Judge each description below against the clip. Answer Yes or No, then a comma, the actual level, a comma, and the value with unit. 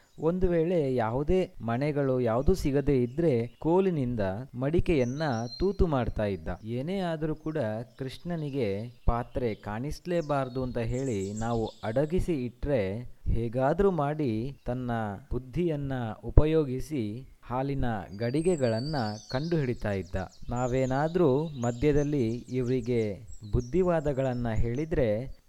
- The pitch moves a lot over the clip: No, average, 4.6 semitones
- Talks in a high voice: No, low, 130 Hz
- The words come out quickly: No, average, 85 wpm